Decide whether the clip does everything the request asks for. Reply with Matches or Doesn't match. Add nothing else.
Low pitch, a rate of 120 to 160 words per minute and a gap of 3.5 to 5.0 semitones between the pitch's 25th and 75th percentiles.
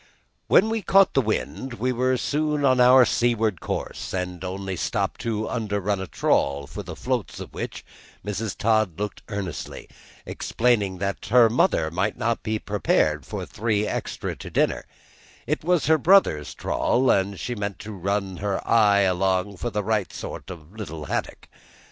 Doesn't match